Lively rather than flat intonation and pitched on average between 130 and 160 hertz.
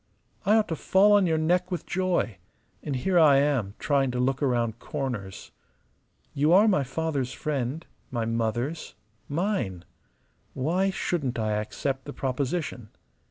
Yes: wide, 5.9 semitones; medium, 140 Hz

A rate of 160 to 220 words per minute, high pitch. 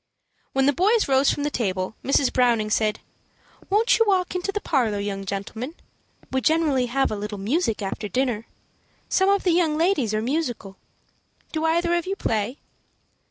Yes: average, 170 wpm; very high, 265 Hz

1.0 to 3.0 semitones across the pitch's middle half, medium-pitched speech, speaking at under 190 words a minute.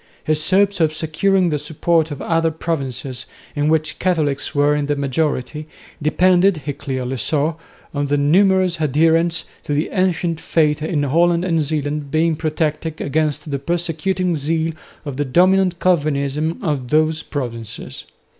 Yes: average, 2.7 semitones; medium, 155 Hz; average, 150 wpm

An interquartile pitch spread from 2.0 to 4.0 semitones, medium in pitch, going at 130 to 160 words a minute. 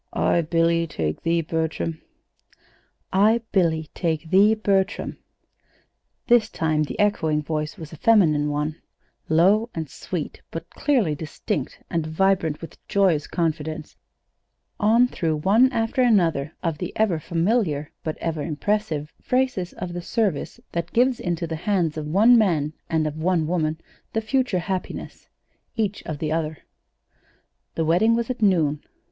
No: average, 4.9 semitones; medium, 170 Hz; average, 145 wpm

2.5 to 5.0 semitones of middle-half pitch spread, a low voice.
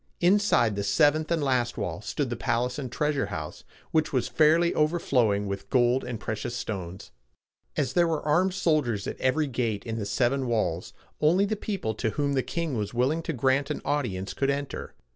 No: wide, 5.6 semitones; low, 130 Hz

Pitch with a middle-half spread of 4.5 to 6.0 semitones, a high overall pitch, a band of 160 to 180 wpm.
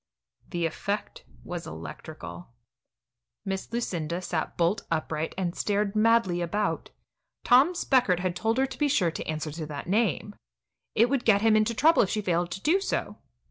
Yes: average, 5.2 semitones; high, 195 Hz; average, 170 wpm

